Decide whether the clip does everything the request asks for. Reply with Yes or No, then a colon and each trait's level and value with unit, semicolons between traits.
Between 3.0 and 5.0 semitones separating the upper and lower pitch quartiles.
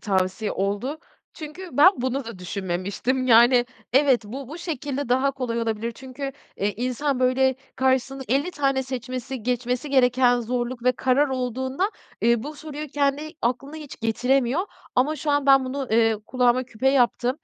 No: narrow, 2.5 semitones